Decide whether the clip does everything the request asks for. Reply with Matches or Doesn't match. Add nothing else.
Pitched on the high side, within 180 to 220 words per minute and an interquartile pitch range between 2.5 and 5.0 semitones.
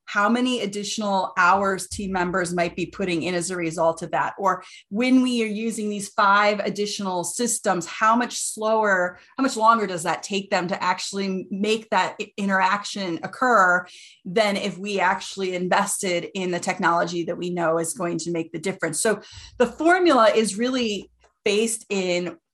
Doesn't match